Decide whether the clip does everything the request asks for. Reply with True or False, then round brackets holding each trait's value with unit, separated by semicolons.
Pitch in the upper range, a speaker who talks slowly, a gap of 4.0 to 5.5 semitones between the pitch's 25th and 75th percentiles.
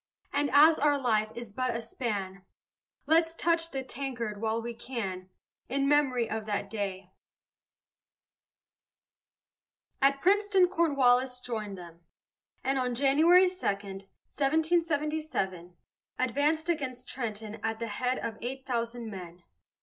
True (250 Hz; 120 wpm; 5.2 semitones)